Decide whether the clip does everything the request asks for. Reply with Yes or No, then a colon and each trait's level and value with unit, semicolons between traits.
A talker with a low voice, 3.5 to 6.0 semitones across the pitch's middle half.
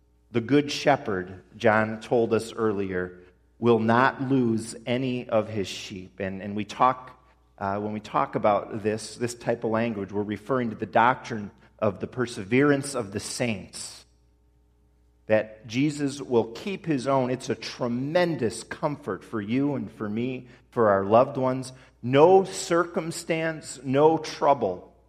Yes: low, 115 Hz; average, 4.2 semitones